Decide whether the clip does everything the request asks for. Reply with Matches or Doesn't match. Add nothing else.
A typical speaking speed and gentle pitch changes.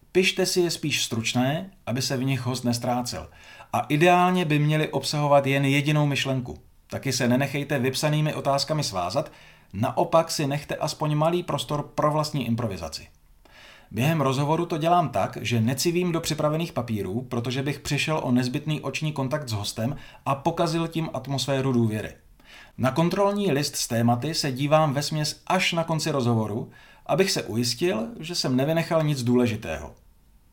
Doesn't match